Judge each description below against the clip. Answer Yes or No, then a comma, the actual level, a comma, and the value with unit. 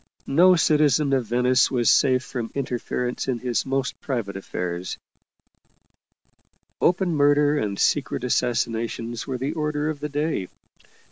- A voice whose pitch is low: Yes, low, 130 Hz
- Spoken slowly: Yes, slow, 130 wpm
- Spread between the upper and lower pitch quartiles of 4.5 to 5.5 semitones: No, average, 3.7 semitones